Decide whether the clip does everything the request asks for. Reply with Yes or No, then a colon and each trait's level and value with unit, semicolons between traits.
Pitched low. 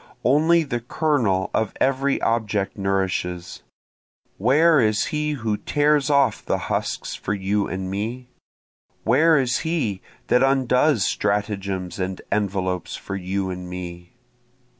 Yes: low, 105 Hz